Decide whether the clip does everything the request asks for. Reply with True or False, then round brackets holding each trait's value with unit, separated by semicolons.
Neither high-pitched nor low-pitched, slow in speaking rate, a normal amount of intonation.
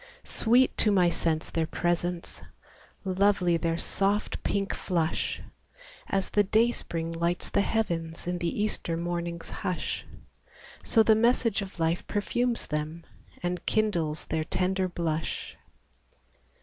True (175 Hz; 100 wpm; 3.6 semitones)